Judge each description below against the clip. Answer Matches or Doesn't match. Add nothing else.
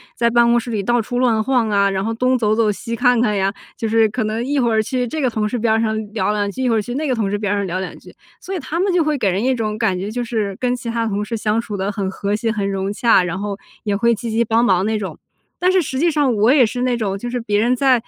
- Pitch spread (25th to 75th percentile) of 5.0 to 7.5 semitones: Doesn't match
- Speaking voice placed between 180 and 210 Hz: Doesn't match